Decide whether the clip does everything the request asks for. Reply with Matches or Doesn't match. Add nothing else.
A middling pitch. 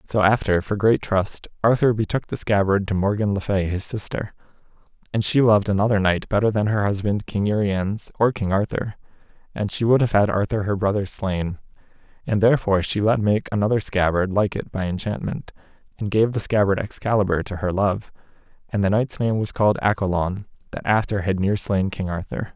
Doesn't match